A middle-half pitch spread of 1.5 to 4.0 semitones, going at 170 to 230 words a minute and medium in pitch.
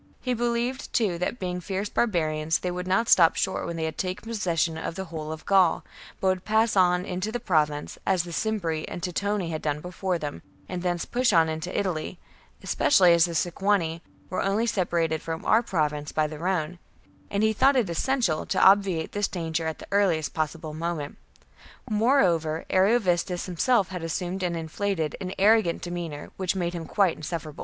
Yes: average, 3.6 semitones; average, 185 wpm; medium, 180 Hz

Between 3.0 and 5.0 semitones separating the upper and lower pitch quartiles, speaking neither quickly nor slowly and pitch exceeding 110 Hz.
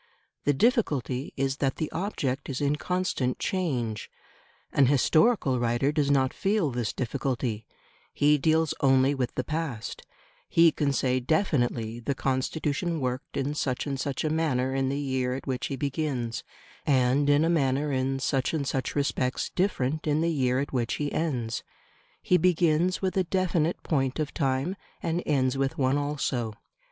Yes: average, 3.4 semitones; average, 165 wpm; medium, 140 Hz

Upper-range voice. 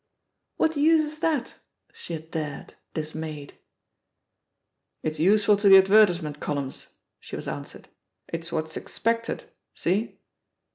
No: medium, 175 Hz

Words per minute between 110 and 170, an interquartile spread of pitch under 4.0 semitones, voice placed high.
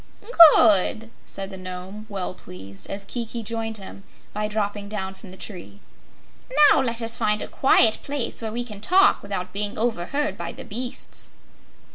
Yes: average, 165 wpm; average, 3.1 semitones; high, 210 Hz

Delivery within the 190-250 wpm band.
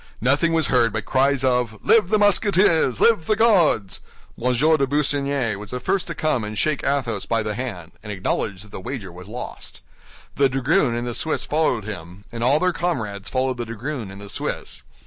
Yes: average, 200 wpm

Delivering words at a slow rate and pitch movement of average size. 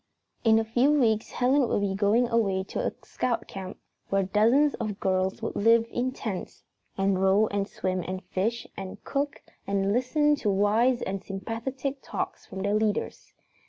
No: average, 170 wpm; average, 4.0 semitones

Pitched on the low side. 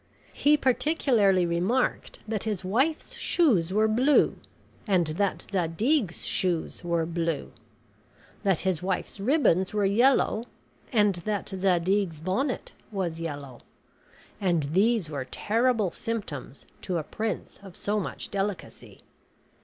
No: high, 195 Hz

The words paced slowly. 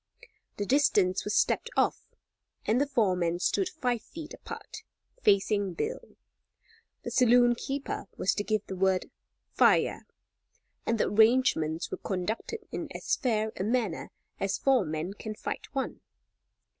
No: average, 145 wpm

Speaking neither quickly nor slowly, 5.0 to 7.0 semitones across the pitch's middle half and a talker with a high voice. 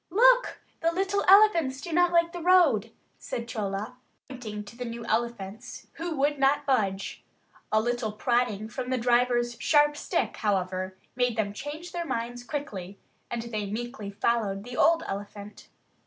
Yes: average, 155 wpm; wide, 5.6 semitones; high, 240 Hz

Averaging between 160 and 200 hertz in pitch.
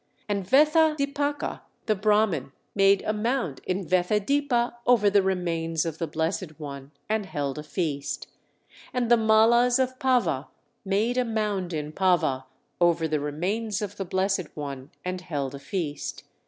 Yes: high, 190 Hz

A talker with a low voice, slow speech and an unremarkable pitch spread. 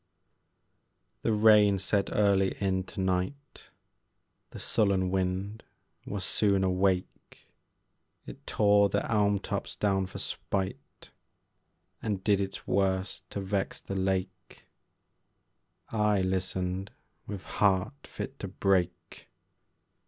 No: very low, 95 Hz; slow, 110 wpm; narrow, 1.5 semitones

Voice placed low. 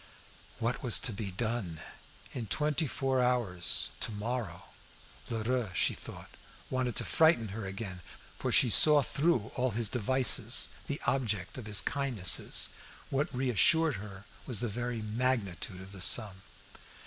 Yes: low, 115 Hz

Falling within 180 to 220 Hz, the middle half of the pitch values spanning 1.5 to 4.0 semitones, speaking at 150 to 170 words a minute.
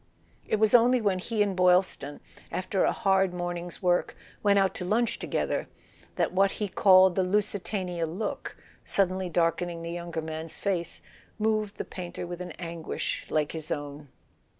Yes: medium, 185 Hz; average, 2.7 semitones; average, 165 wpm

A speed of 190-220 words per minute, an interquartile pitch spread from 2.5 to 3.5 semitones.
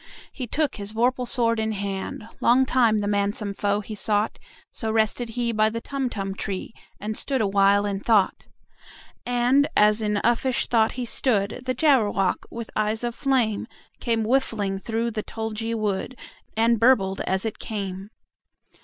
No: average, 160 wpm; average, 2.8 semitones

